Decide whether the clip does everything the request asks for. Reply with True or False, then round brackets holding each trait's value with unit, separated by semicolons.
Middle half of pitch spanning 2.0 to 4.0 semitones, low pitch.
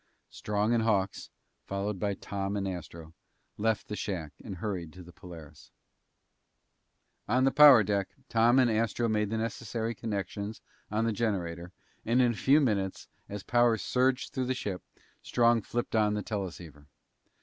True (3.3 semitones; 105 Hz)